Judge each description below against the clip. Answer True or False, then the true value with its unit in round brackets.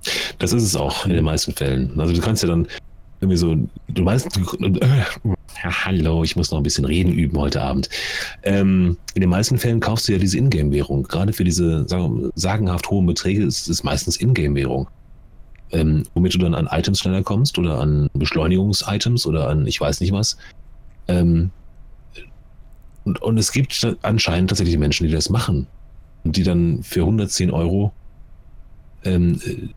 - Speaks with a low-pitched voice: True (90 Hz)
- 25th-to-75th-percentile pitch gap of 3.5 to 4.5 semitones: True (3.8 semitones)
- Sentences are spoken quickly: False (165 wpm)